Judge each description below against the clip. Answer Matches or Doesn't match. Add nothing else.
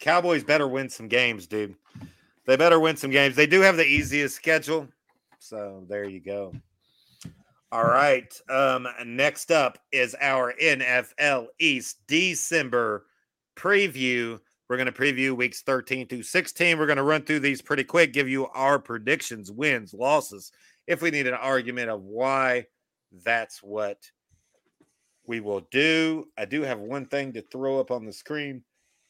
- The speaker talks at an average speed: Matches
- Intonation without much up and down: Doesn't match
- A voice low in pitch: Matches